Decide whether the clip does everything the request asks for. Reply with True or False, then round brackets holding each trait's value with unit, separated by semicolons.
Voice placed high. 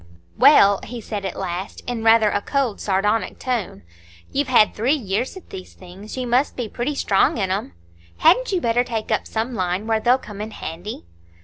True (220 Hz)